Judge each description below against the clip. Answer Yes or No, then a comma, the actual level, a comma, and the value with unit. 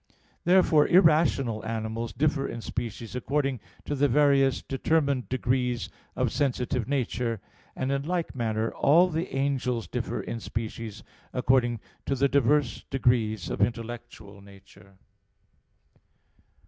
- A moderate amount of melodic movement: Yes, average, 3.6 semitones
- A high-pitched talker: No, low, 125 Hz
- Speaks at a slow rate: Yes, slow, 120 wpm